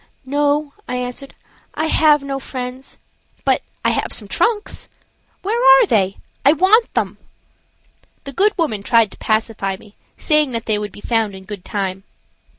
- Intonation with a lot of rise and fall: Yes, wide, 6.2 semitones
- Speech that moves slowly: No, average, 160 wpm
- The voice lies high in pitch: Yes, very high, 260 Hz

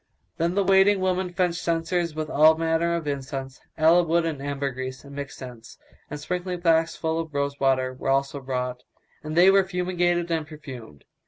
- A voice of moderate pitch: Yes, medium, 160 Hz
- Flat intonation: No, average, 4.1 semitones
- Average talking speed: Yes, average, 180 wpm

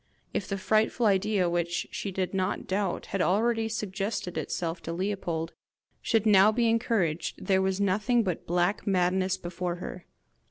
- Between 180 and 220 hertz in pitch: Yes, high, 190 Hz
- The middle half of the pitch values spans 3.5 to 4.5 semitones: No, average, 2.9 semitones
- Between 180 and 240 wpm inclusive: No, average, 155 wpm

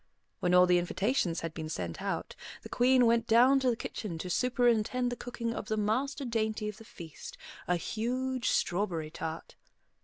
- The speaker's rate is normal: Yes, average, 180 wpm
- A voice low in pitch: No, high, 220 Hz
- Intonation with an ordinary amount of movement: No, wide, 5.7 semitones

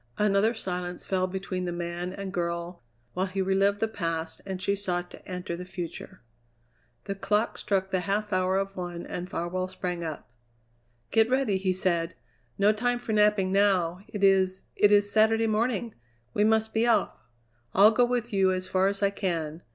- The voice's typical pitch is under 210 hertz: Yes, high, 190 Hz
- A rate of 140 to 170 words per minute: No, average, 180 wpm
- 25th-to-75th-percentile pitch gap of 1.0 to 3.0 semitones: Yes, narrow, 2.6 semitones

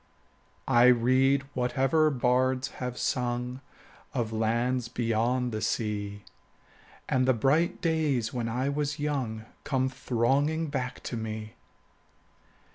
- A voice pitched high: No, low, 125 Hz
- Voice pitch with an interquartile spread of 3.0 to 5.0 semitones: No, narrow, 2.6 semitones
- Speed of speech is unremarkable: No, slow, 120 wpm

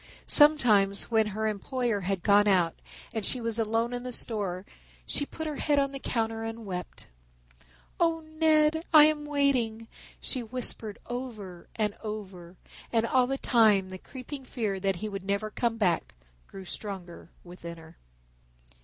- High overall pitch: Yes, high, 225 Hz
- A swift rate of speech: No, average, 160 wpm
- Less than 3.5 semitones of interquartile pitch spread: No, average, 4.6 semitones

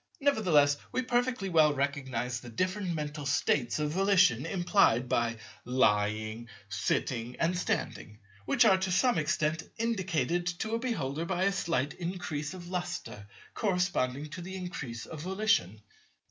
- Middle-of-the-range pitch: Yes, medium, 160 Hz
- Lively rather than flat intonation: Yes, wide, 6.8 semitones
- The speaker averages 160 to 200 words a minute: No, average, 140 wpm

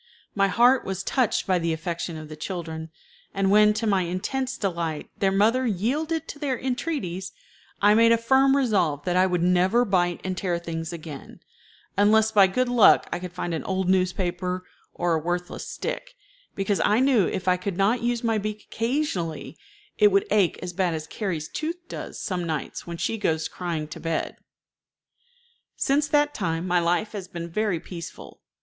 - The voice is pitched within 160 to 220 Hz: Yes, high, 190 Hz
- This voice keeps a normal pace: Yes, average, 180 wpm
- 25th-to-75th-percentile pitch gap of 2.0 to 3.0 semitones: No, average, 4.7 semitones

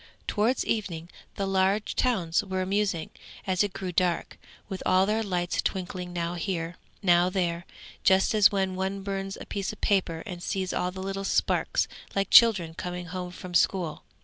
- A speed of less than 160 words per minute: No, average, 175 wpm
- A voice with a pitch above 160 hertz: Yes, high, 190 Hz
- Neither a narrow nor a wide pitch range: No, narrow, 1.9 semitones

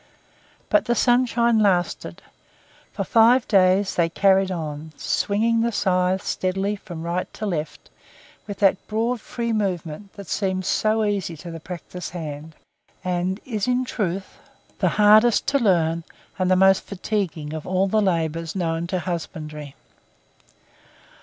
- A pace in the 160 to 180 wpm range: No, average, 140 wpm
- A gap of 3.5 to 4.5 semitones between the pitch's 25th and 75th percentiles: Yes, average, 3.9 semitones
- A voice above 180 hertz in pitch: Yes, high, 190 Hz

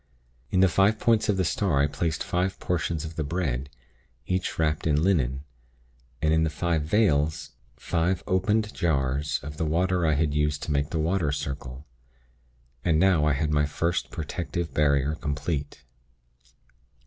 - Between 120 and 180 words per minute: Yes, average, 160 wpm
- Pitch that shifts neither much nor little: Yes, average, 3.5 semitones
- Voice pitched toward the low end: Yes, very low, 80 Hz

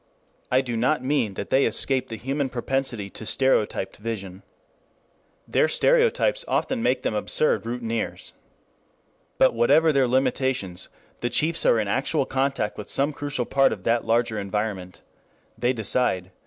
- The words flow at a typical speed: Yes, average, 145 wpm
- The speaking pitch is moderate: No, low, 125 Hz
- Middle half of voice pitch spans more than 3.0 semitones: Yes, average, 3.9 semitones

